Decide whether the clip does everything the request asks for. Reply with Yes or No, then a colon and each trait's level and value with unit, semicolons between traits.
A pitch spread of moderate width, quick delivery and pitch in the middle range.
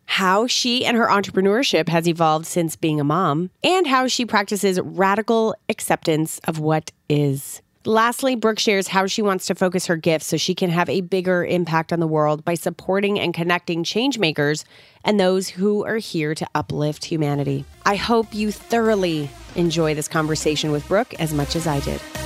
No: average, 4.7 semitones; average, 180 wpm; medium, 175 Hz